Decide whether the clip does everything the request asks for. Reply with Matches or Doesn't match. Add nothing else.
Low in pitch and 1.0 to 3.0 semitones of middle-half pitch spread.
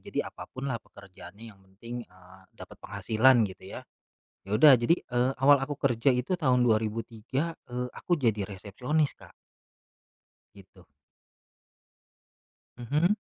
Doesn't match